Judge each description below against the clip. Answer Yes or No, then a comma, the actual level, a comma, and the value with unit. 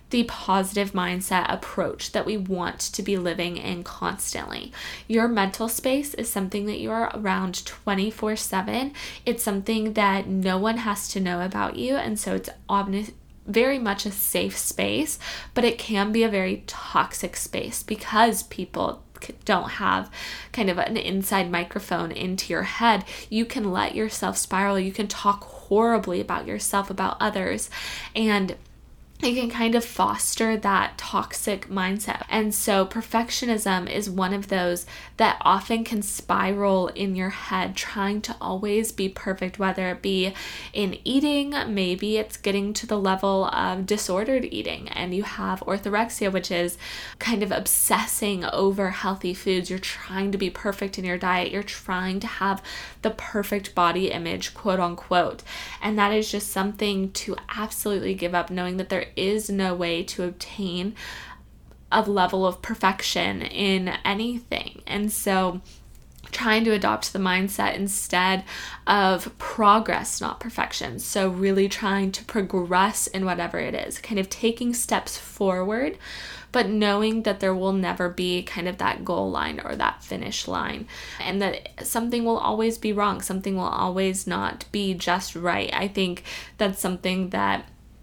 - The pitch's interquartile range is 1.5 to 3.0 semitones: Yes, narrow, 2.5 semitones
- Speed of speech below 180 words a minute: Yes, average, 155 wpm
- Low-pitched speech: No, high, 195 Hz